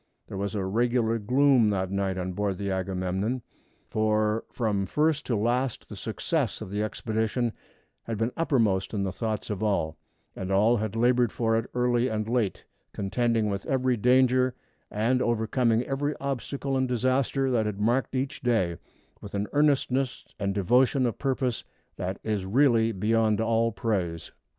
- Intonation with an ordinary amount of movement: Yes, average, 3.8 semitones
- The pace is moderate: Yes, average, 160 wpm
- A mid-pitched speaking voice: No, low, 115 Hz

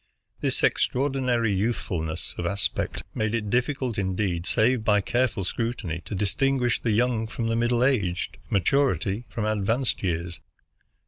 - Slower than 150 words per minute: Yes, average, 140 wpm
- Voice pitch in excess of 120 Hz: No, low, 110 Hz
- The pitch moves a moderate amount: Yes, average, 4.0 semitones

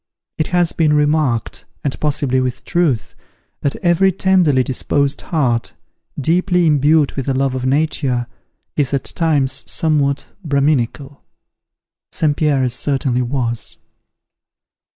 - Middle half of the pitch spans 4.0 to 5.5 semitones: No, average, 3.2 semitones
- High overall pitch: No, medium, 145 Hz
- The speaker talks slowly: Yes, slow, 115 wpm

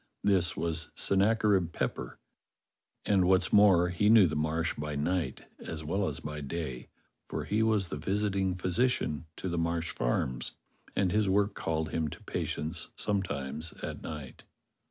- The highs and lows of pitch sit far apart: No, average, 4.3 semitones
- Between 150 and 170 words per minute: Yes, average, 155 wpm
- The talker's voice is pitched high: No, very low, 85 Hz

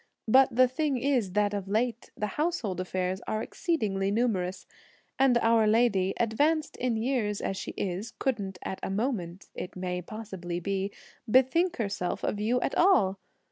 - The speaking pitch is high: Yes, high, 215 Hz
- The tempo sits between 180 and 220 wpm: No, average, 155 wpm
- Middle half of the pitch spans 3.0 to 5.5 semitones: Yes, average, 4.6 semitones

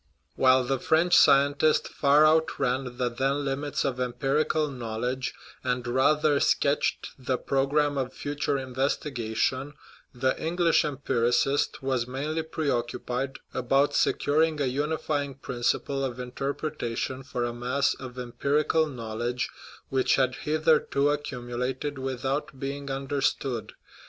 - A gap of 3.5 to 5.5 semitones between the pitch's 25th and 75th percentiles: No, narrow, 2.5 semitones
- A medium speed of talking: No, slow, 120 wpm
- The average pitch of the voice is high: No, low, 135 Hz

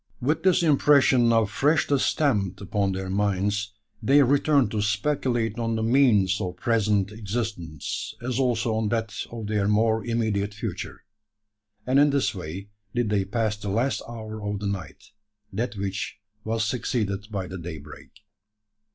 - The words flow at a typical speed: Yes, average, 150 wpm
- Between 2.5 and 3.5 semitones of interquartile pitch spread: Yes, average, 3.2 semitones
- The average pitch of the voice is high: No, low, 110 Hz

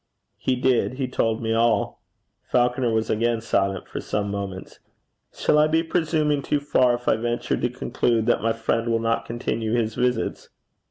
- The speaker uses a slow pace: No, average, 175 wpm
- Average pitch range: No, narrow, 2.2 semitones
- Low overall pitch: Yes, low, 120 Hz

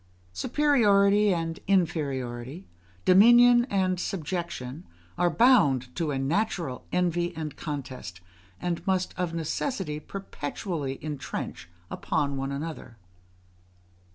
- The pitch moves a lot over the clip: Yes, wide, 5.7 semitones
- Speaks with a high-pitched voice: No, medium, 170 Hz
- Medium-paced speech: No, slow, 100 wpm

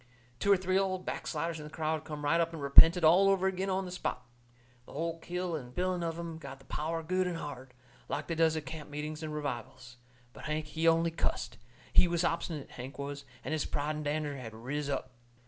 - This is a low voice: No, medium, 155 Hz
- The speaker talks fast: Yes, fast, 225 wpm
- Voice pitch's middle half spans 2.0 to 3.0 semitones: Yes, average, 2.7 semitones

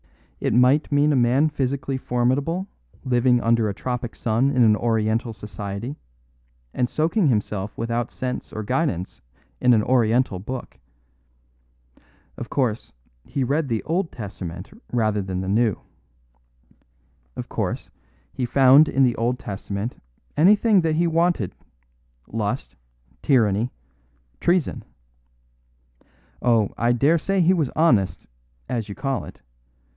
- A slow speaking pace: Yes, slow, 130 wpm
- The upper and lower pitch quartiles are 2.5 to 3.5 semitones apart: No, average, 4.7 semitones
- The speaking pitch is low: Yes, low, 125 Hz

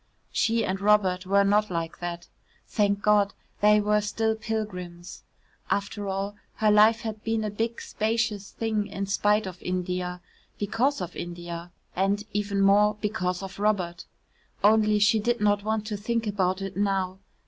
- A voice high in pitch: Yes, high, 205 Hz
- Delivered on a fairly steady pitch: Yes, narrow, 2.1 semitones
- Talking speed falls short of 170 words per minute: Yes, average, 160 wpm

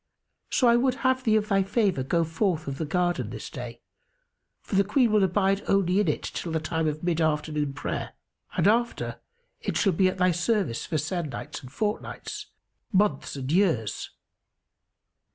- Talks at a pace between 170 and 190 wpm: Yes, average, 175 wpm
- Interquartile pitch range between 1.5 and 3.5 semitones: No, average, 5.0 semitones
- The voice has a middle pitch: Yes, medium, 180 Hz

